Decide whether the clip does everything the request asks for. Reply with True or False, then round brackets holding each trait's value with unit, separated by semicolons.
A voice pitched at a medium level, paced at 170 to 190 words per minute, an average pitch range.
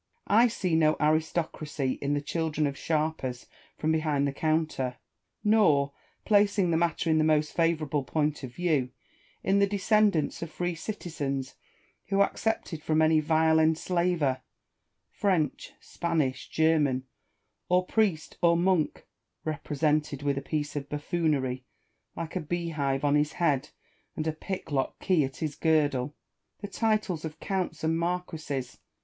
False (155 Hz; 145 wpm; 3.0 semitones)